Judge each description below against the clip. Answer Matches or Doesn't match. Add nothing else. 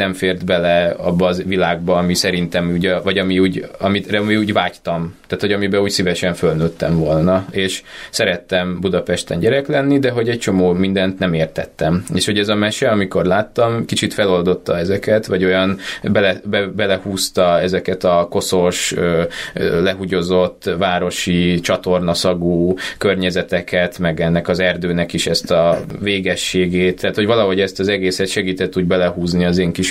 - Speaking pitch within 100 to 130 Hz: Doesn't match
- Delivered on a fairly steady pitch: Matches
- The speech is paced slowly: Doesn't match